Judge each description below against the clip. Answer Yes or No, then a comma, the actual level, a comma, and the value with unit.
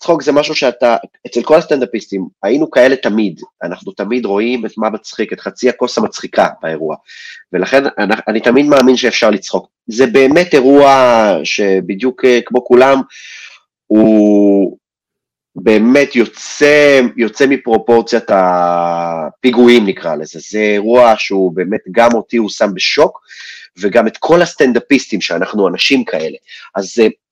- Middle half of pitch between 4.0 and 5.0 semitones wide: Yes, average, 4.7 semitones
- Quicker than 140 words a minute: No, average, 130 wpm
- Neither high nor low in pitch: No, low, 115 Hz